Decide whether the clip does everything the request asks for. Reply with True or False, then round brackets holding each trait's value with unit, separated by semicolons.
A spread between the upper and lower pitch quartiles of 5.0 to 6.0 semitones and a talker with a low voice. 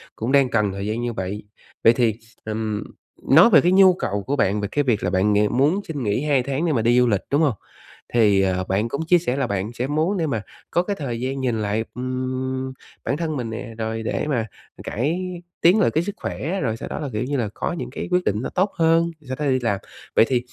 True (5.3 semitones; 125 Hz)